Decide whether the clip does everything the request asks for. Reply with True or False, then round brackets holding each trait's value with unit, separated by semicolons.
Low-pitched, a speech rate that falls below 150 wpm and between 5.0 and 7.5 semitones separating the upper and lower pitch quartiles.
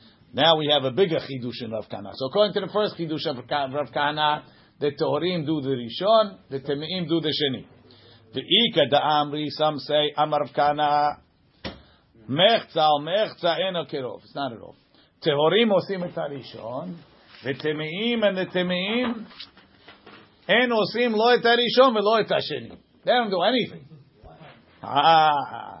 False (150 Hz; 140 wpm; 5.5 semitones)